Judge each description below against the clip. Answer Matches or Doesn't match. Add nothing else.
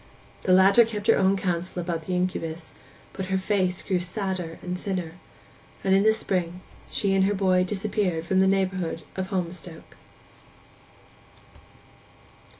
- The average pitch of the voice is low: Doesn't match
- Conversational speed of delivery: Matches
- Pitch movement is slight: Matches